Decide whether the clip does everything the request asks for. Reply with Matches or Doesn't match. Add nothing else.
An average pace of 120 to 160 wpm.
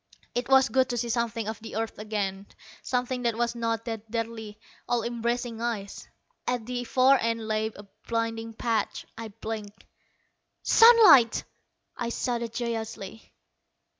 Matches